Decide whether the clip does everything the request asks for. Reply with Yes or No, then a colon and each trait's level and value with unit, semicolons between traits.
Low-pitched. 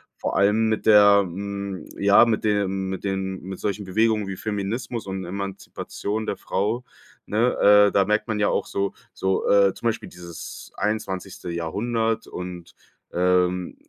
Yes: low, 100 Hz